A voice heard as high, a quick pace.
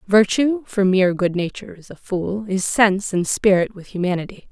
No: high, 195 Hz; average, 185 wpm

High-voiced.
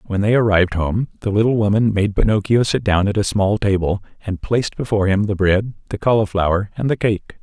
No: low, 105 Hz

